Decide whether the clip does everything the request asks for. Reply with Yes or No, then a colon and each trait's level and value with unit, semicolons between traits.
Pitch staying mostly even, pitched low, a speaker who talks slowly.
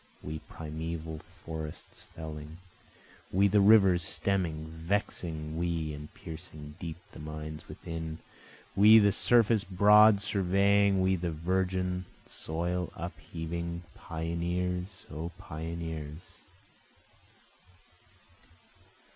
No: average, 3.0 semitones; very low, 85 Hz; slow, 90 wpm